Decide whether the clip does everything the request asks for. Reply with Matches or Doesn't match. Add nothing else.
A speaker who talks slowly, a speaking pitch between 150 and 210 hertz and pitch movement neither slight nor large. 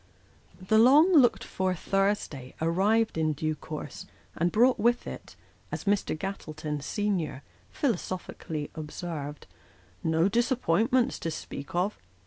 Doesn't match